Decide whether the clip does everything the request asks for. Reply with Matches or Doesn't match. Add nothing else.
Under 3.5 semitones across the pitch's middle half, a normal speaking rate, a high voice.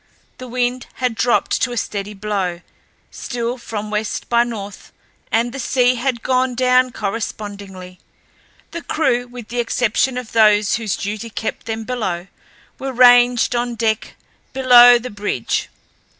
Matches